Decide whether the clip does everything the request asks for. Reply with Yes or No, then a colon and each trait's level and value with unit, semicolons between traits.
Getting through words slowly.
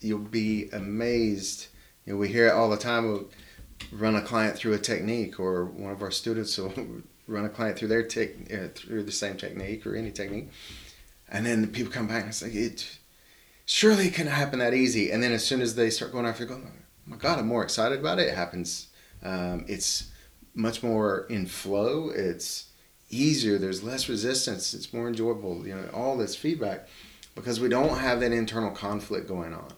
No: fast, 205 wpm